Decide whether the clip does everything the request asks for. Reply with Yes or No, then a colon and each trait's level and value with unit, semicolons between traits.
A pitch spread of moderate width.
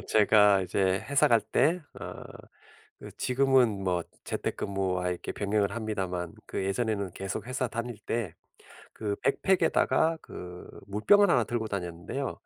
Yes: average, 4.3 semitones